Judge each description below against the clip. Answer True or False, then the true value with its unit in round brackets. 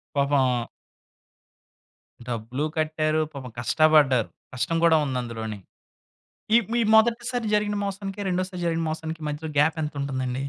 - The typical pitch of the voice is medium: True (155 Hz)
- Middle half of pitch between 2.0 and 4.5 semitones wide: False (5.3 semitones)